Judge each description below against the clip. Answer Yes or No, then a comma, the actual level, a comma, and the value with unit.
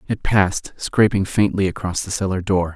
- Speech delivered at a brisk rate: No, average, 175 wpm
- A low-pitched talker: Yes, very low, 95 Hz